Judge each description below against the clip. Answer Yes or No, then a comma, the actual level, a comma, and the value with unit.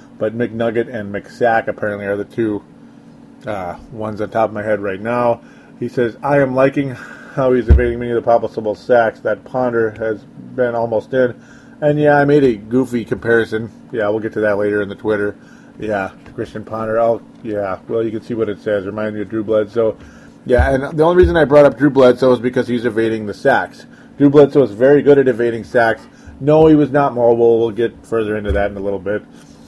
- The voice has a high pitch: No, low, 115 Hz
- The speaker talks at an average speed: No, fast, 215 wpm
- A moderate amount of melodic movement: Yes, average, 3.3 semitones